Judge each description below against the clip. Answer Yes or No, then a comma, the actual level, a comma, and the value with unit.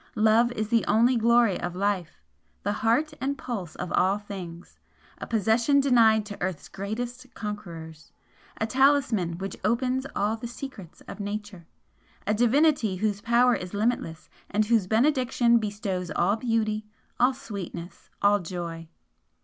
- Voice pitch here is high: Yes, high, 215 Hz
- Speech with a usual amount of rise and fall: Yes, average, 4.0 semitones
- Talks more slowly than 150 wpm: Yes, average, 140 wpm